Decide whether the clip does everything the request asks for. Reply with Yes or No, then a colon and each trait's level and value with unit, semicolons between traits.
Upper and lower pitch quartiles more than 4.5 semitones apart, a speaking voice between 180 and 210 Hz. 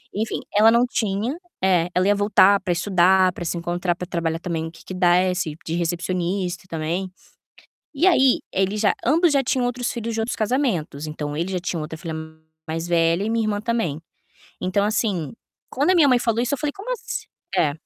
Yes: average, 5.2 semitones; high, 190 Hz